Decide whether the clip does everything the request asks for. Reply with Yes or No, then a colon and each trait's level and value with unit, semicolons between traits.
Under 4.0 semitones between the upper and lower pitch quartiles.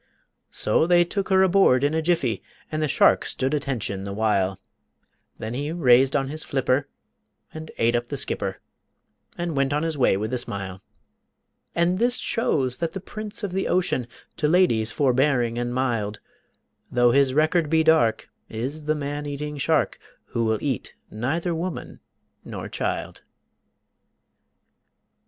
No: average, 5.1 semitones